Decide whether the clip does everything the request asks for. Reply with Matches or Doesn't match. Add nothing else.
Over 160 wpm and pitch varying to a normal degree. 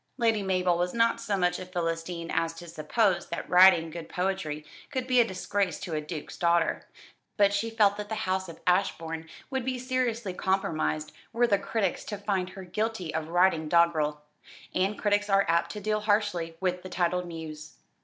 Matches